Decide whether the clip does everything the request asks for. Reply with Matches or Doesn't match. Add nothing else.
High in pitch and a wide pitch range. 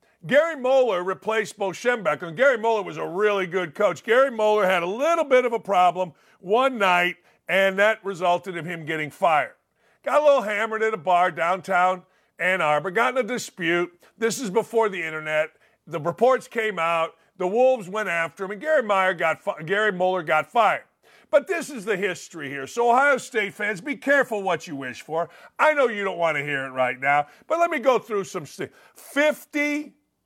Matches